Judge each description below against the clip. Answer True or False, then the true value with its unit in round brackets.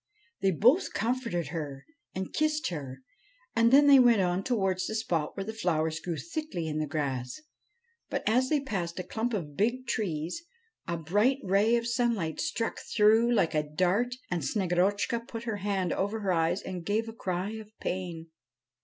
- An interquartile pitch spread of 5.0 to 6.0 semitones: True (5.5 semitones)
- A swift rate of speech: False (180 wpm)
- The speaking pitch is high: True (195 Hz)